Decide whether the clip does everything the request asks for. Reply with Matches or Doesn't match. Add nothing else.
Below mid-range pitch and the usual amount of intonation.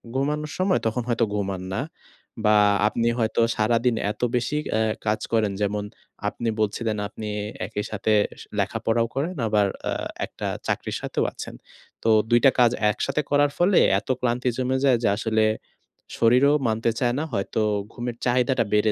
Matches